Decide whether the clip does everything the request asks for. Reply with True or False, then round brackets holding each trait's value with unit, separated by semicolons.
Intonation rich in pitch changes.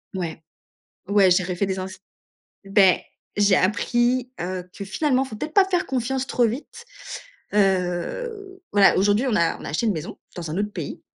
True (5.7 semitones)